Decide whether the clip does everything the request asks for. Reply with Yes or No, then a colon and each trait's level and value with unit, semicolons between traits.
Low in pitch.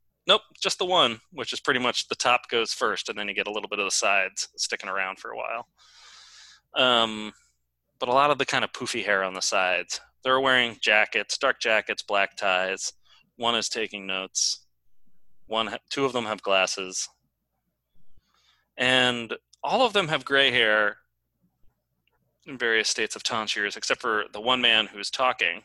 Yes: low, 125 Hz